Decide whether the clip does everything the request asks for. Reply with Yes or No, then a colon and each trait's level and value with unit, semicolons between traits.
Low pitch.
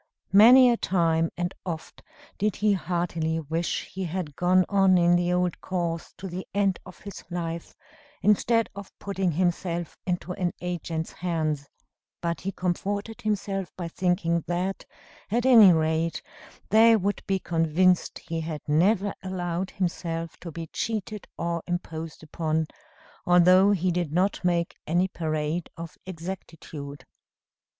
No: medium, 175 Hz